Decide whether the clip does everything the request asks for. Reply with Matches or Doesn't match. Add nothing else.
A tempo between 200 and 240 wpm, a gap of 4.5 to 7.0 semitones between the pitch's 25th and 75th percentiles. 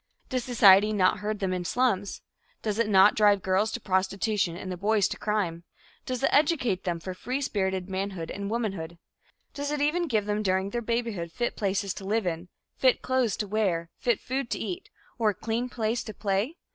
Doesn't match